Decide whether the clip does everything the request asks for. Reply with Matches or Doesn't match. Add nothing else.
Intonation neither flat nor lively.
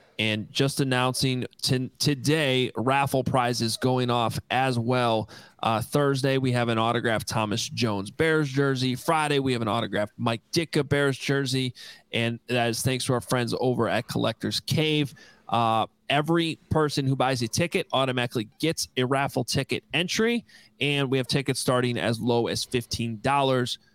Matches